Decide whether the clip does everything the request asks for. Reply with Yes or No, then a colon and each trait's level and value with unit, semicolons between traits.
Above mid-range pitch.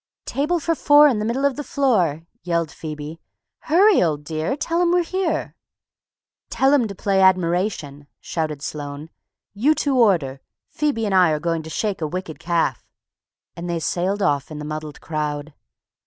No: medium, 175 Hz